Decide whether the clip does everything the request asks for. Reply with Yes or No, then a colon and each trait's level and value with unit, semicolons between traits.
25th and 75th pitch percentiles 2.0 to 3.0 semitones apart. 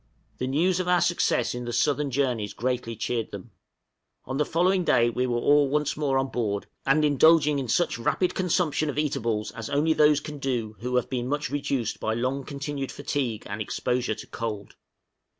No: average, 3.9 semitones